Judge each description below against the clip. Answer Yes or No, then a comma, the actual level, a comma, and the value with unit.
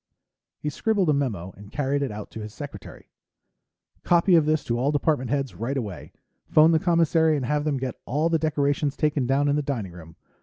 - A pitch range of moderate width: Yes, average, 4.3 semitones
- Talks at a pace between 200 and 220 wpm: Yes, fast, 205 wpm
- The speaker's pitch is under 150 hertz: Yes, medium, 140 Hz